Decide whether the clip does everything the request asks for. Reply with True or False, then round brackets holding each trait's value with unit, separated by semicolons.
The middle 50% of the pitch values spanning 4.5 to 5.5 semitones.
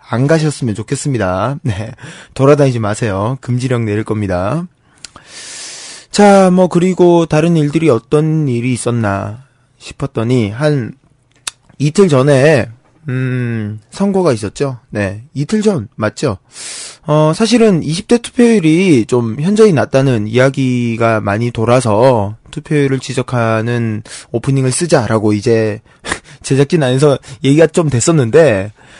True (5.1 semitones)